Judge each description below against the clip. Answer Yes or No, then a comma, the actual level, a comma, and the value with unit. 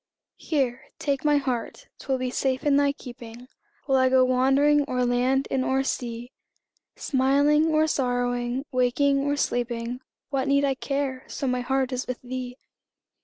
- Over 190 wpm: No, average, 160 wpm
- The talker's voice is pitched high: Yes, very high, 260 Hz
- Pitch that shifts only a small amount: Yes, narrow, 2.0 semitones